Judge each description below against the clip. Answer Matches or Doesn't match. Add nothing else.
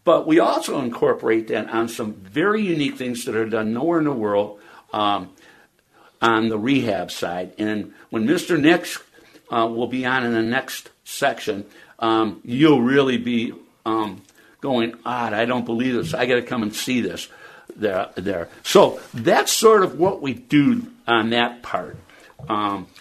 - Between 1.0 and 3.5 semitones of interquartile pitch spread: Matches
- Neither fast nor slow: Matches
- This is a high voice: Doesn't match